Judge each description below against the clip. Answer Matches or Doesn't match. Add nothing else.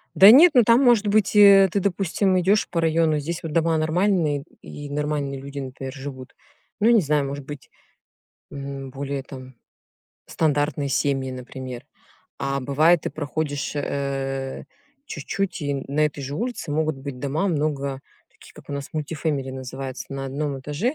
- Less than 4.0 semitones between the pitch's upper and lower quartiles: Matches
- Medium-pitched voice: Matches